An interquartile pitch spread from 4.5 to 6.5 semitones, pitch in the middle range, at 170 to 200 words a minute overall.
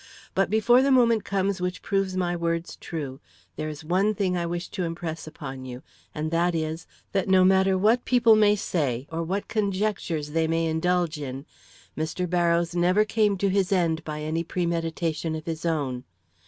No: average, 3.4 semitones; medium, 175 Hz; average, 180 wpm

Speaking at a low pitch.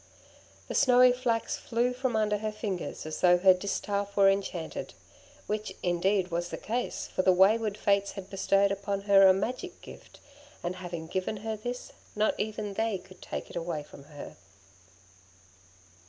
No: high, 200 Hz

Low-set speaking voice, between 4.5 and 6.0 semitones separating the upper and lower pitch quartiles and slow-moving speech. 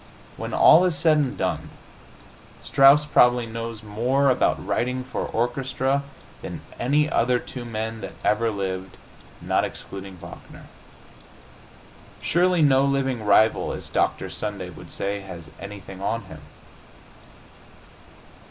Yes: low, 115 Hz; average, 5.0 semitones; slow, 125 wpm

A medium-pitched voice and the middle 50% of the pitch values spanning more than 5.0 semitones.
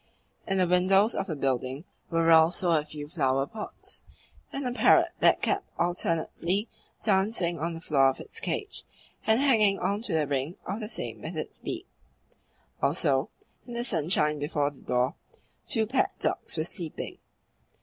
Yes: medium, 170 Hz; wide, 5.4 semitones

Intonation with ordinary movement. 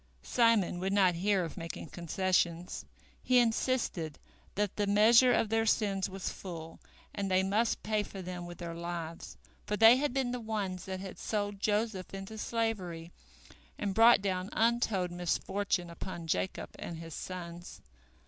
Yes: average, 3.8 semitones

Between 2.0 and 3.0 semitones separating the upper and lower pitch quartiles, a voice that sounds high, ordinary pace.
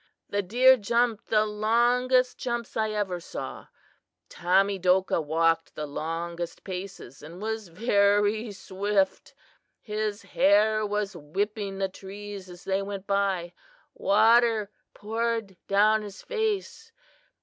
No: narrow, 2.6 semitones; high, 205 Hz; slow, 115 wpm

